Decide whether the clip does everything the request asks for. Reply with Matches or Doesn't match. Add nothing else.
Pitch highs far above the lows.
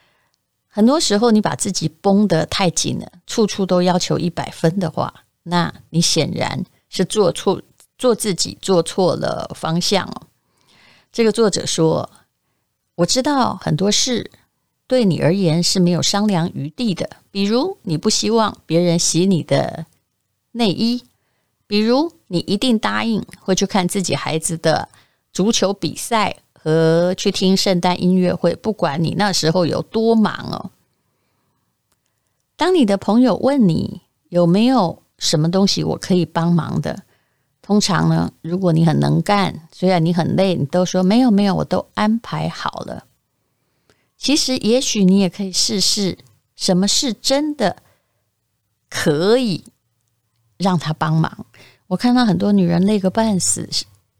Doesn't match